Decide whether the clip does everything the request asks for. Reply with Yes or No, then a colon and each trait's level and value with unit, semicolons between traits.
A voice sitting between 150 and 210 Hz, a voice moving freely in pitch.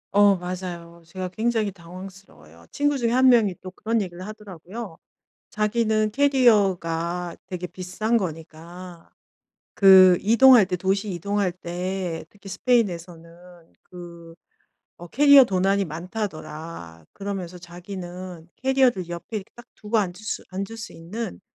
No: medium, 185 Hz; average, 3.7 semitones